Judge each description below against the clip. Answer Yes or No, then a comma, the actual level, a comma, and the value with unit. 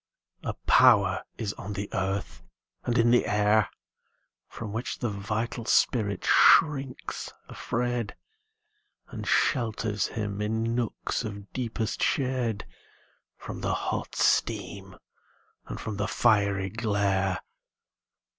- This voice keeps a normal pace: No, slow, 110 wpm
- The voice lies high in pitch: No, low, 110 Hz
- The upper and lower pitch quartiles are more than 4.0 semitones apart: No, average, 2.7 semitones